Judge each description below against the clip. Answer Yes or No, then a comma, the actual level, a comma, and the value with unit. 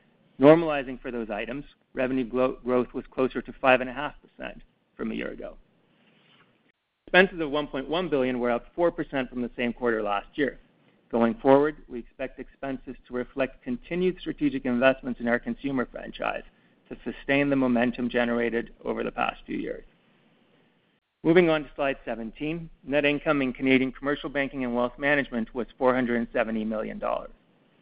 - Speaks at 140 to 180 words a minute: Yes, average, 145 wpm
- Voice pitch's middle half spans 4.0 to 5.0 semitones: No, average, 3.0 semitones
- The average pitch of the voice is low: Yes, low, 130 Hz